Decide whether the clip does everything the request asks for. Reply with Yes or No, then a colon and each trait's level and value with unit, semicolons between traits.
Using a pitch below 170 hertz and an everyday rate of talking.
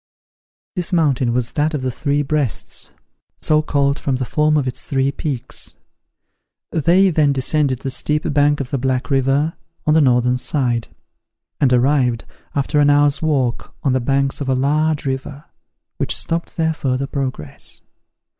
Yes: medium, 140 Hz; average, 160 wpm